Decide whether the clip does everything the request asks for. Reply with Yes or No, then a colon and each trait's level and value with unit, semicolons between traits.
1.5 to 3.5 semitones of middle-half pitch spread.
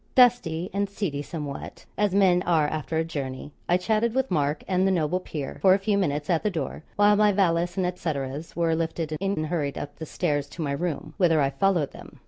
No: average, 4.4 semitones